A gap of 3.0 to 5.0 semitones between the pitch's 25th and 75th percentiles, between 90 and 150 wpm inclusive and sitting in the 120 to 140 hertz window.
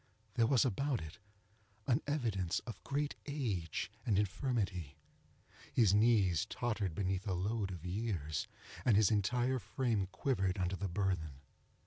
No: average, 4.7 semitones; slow, 135 wpm; low, 100 Hz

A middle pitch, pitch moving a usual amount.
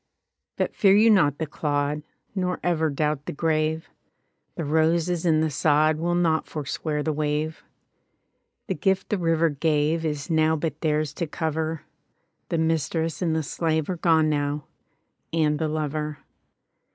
No: medium, 155 Hz; narrow, 1.5 semitones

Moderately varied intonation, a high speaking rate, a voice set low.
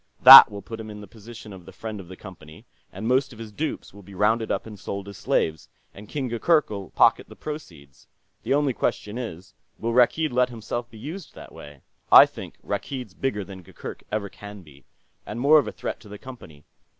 Yes: average, 4.3 semitones; fast, 215 wpm; low, 105 Hz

